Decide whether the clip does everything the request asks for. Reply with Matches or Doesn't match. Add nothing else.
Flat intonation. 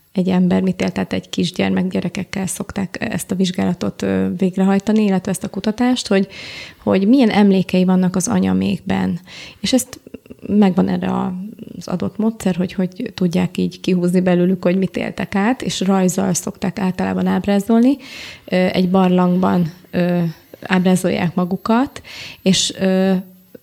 Matches